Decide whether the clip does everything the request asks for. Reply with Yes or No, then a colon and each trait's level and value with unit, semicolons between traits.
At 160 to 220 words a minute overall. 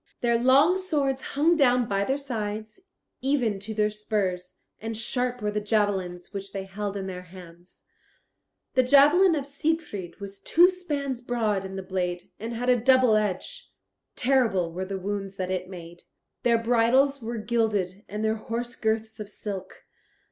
Yes: average, 165 wpm